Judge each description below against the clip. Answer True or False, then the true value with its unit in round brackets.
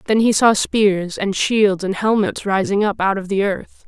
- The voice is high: True (200 Hz)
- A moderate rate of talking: False (215 wpm)